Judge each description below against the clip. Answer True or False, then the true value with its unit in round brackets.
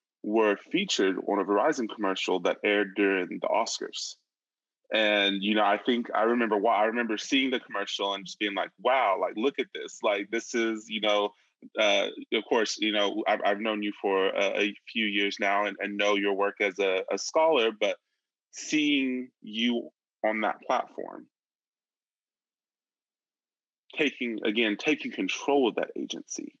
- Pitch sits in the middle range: False (110 Hz)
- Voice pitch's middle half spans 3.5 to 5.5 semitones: True (4.2 semitones)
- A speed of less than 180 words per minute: True (170 wpm)